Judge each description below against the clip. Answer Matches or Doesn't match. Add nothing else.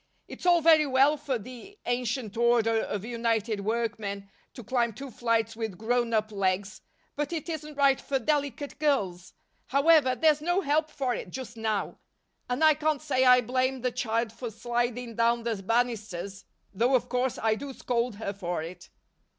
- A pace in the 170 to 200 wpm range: Matches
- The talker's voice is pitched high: Matches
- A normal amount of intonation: Matches